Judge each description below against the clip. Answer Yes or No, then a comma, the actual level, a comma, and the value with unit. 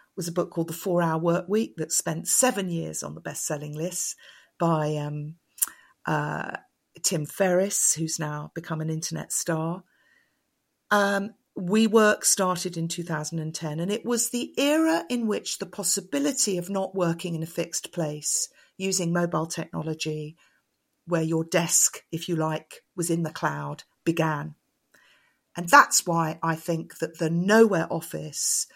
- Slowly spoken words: No, average, 150 wpm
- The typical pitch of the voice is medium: Yes, medium, 170 Hz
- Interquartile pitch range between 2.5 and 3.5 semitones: Yes, average, 3.1 semitones